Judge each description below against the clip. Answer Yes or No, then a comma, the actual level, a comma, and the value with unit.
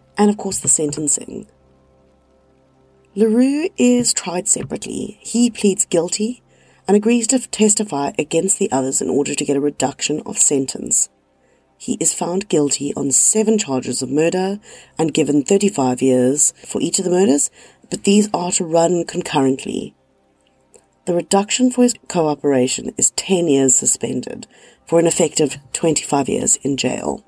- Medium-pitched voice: Yes, medium, 165 Hz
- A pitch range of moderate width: No, wide, 6.8 semitones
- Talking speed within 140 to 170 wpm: Yes, average, 145 wpm